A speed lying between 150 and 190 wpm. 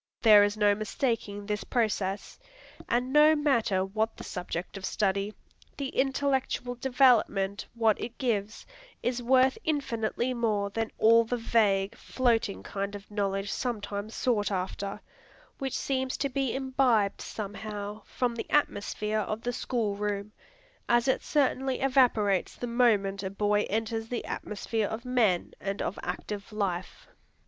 No: average, 140 wpm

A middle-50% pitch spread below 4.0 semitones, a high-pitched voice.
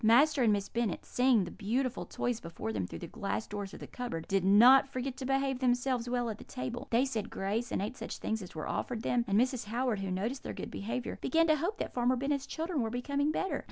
No: average, 4.3 semitones; high, 245 Hz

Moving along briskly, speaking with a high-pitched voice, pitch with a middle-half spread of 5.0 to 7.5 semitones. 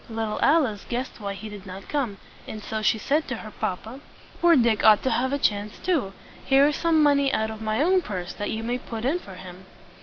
Yes: fast, 235 wpm; high, 225 Hz; average, 5.3 semitones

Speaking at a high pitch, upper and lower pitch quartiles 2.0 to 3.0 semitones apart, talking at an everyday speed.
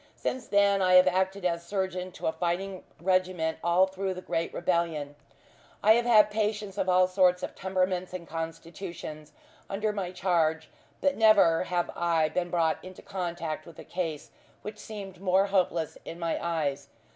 No: medium, 180 Hz; narrow, 2.4 semitones; average, 170 wpm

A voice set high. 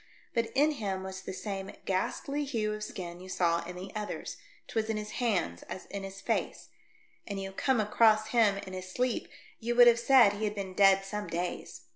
Yes: high, 205 Hz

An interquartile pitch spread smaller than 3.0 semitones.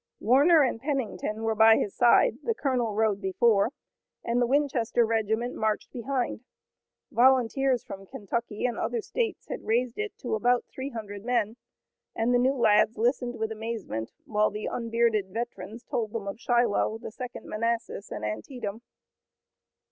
Yes: narrow, 2.5 semitones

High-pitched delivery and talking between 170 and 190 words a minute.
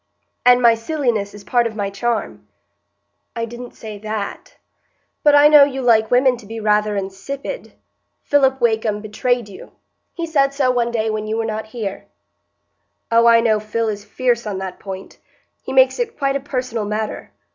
Yes: high, 230 Hz; average, 180 wpm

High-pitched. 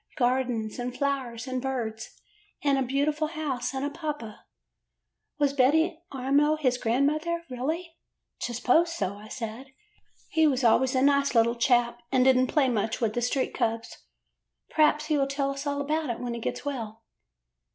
Yes: very high, 265 Hz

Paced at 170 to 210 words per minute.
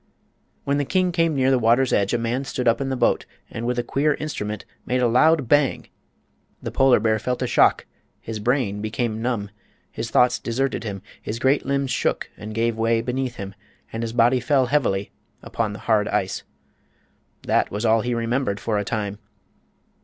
Yes: average, 190 wpm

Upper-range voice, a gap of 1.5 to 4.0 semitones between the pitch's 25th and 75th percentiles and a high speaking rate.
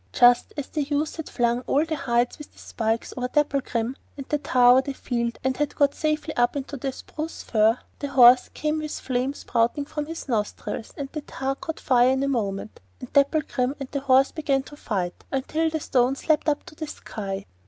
Yes: very high, 270 Hz; average, 3.5 semitones; fast, 210 wpm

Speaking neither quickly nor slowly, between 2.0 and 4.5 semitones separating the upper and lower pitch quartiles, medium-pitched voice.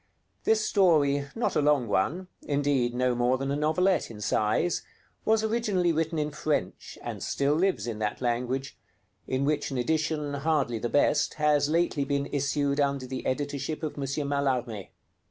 Yes: average, 165 wpm; average, 3.3 semitones; medium, 145 Hz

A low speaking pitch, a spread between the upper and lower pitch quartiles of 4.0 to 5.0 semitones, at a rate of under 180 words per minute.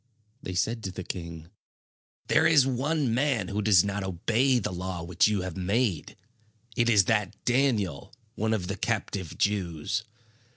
Yes: low, 100 Hz; average, 4.4 semitones; average, 160 wpm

